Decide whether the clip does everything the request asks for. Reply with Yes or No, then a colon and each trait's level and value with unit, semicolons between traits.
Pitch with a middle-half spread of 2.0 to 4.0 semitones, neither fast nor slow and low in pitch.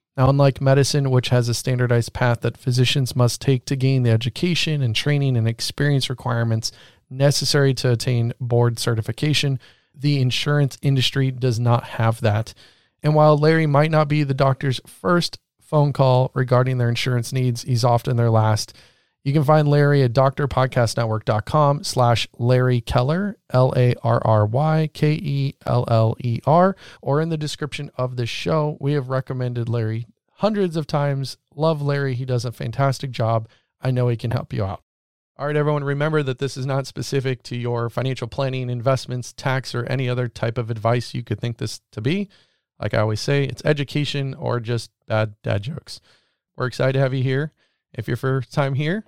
Yes: average, 3.1 semitones; average, 180 wpm; low, 130 Hz